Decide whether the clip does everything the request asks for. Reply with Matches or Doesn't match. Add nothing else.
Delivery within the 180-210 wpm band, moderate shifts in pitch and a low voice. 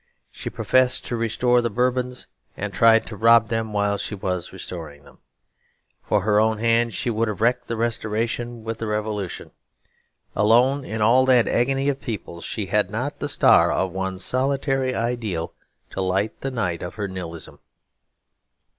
Doesn't match